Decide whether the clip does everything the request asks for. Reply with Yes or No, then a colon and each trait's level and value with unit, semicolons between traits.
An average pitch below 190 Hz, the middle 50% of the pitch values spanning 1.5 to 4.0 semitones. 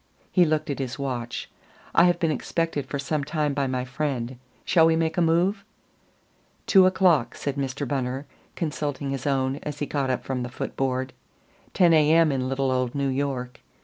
Yes: medium, 140 Hz; average, 3.4 semitones